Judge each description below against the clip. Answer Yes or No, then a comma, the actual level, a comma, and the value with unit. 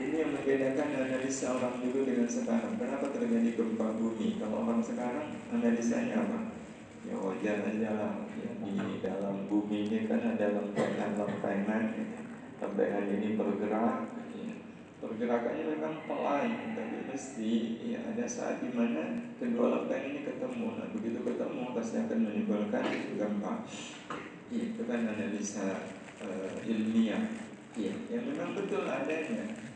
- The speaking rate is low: No, average, 130 wpm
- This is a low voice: No, high, 235 Hz